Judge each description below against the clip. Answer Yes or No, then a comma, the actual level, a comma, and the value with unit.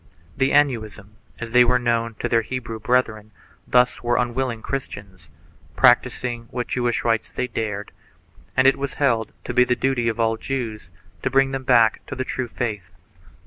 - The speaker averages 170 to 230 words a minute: Yes, average, 175 wpm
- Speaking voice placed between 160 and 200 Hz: No, low, 120 Hz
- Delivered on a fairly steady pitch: Yes, narrow, 2.2 semitones